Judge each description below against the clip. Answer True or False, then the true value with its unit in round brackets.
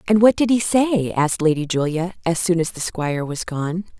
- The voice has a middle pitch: True (175 Hz)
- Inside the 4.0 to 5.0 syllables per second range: False (5.4 syllables/s)